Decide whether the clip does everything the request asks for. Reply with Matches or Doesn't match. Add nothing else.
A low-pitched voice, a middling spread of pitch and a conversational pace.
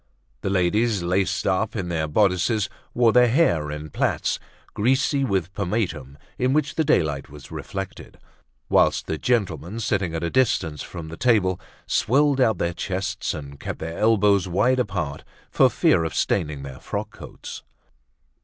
Doesn't match